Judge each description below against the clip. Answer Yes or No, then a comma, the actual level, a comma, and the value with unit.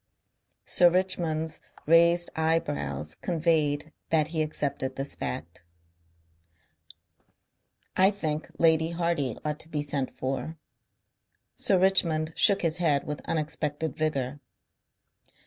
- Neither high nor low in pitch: Yes, medium, 155 Hz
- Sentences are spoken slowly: Yes, slow, 105 wpm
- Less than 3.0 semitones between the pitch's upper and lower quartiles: Yes, narrow, 2.4 semitones